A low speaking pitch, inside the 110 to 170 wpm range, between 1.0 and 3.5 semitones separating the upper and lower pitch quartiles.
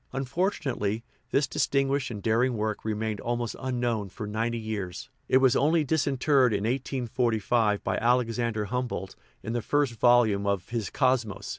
Yes: low, 120 Hz; average, 145 wpm; average, 3.2 semitones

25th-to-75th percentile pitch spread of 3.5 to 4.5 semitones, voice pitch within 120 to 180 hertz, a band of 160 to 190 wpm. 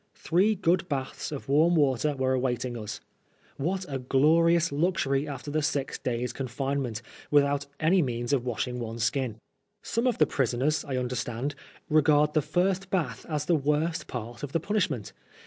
Yes: average, 4.2 semitones; medium, 140 Hz; average, 165 wpm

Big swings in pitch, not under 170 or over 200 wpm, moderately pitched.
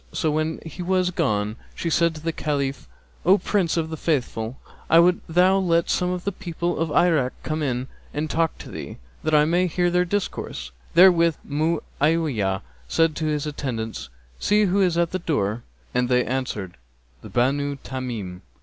No: average, 5.0 semitones; average, 175 wpm; medium, 155 Hz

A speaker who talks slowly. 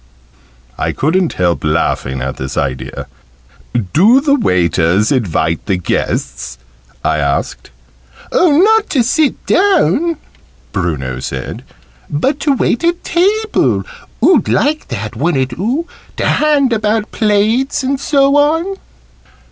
Yes: slow, 120 wpm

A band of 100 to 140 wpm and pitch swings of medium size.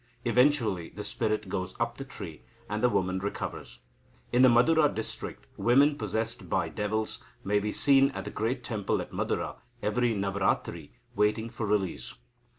No: average, 155 wpm; average, 3.6 semitones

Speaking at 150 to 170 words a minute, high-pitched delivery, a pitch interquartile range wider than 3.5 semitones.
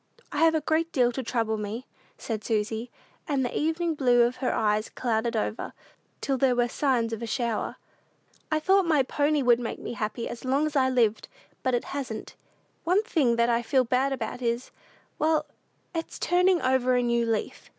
No: average, 190 wpm; very high, 250 Hz; average, 4.0 semitones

